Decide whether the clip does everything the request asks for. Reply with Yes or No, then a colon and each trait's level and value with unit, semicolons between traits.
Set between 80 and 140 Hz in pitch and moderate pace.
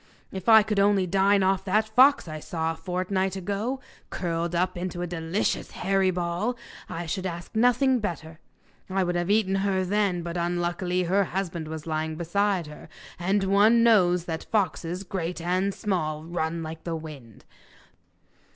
No: medium, 180 Hz; average, 165 wpm